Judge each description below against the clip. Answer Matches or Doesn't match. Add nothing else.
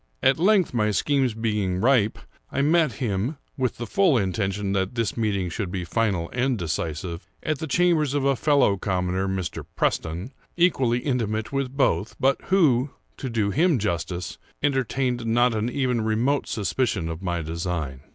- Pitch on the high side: Doesn't match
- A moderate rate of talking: Matches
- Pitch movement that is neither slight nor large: Doesn't match